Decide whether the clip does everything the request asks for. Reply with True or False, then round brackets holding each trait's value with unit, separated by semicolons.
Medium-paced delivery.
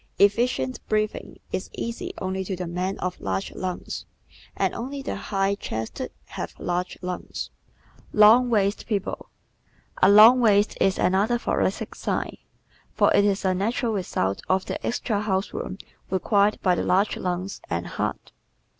True (155 wpm)